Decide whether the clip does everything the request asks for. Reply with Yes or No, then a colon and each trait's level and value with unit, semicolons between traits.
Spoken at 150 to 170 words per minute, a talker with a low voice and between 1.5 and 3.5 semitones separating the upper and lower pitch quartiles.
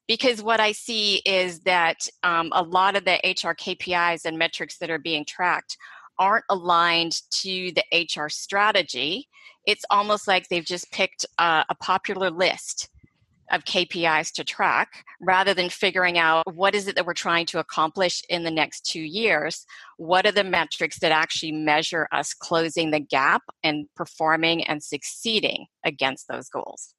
No: average, 165 wpm; medium, 175 Hz; average, 3.0 semitones